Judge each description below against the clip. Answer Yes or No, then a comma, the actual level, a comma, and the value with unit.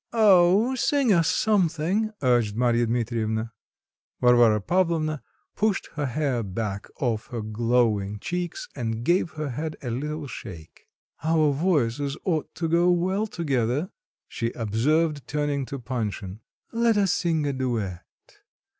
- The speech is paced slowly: Yes, slow, 130 wpm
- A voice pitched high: No, medium, 140 Hz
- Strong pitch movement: Yes, wide, 6.6 semitones